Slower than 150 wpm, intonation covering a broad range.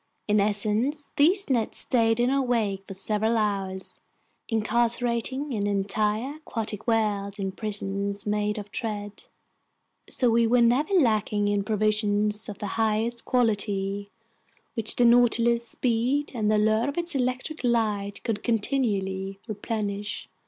No: slow, 135 wpm; average, 2.7 semitones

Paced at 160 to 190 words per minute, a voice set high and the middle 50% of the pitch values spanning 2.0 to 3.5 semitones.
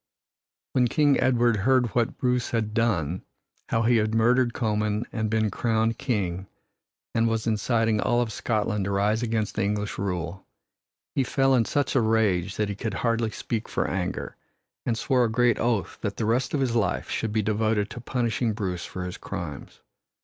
No: average, 185 wpm; low, 110 Hz; narrow, 2.5 semitones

